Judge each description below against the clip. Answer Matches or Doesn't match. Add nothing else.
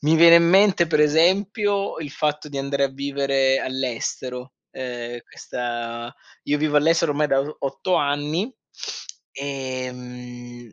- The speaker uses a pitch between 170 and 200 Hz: Doesn't match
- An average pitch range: Matches